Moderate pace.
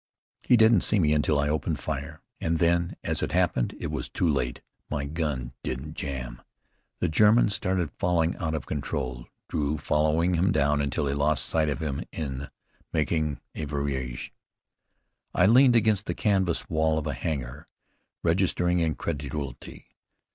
Yes: average, 155 wpm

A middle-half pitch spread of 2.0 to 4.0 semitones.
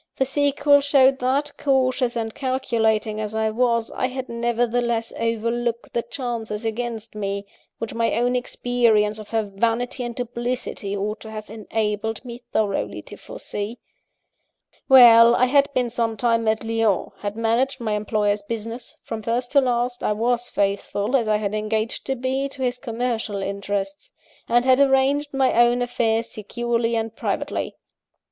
Yes: narrow, 2.4 semitones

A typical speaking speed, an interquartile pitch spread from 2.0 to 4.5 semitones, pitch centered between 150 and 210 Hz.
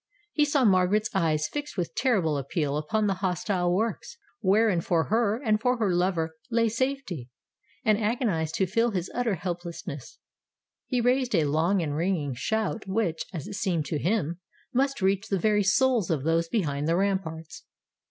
No: average, 170 wpm; wide, 5.4 semitones; high, 190 Hz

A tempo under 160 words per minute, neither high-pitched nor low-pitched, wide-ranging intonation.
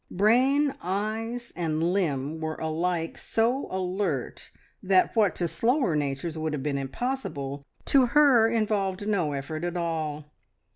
Yes: slow, 135 wpm; medium, 180 Hz; wide, 6.3 semitones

